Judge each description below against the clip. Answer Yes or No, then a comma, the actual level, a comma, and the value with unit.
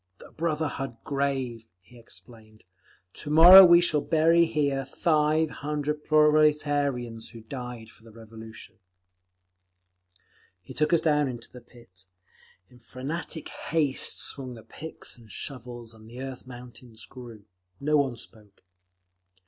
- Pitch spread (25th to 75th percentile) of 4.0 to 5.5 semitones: Yes, average, 4.5 semitones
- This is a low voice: Yes, low, 130 Hz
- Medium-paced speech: No, slow, 125 wpm